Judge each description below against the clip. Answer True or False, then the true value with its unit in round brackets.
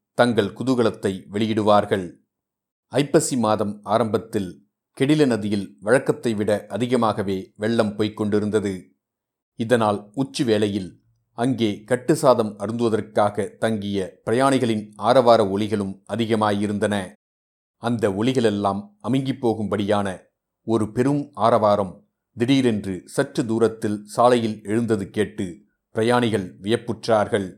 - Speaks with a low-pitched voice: True (110 Hz)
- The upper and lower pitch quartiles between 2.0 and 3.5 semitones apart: True (2.4 semitones)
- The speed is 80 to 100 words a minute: True (85 wpm)